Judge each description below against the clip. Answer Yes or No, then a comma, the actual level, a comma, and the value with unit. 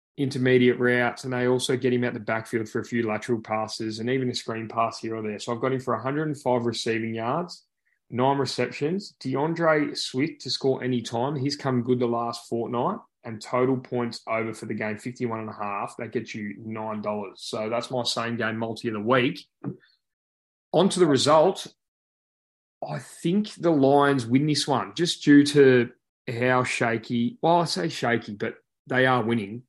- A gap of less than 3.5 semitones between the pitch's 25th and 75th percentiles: Yes, average, 2.9 semitones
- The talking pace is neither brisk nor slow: Yes, average, 190 wpm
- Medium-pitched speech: No, low, 125 Hz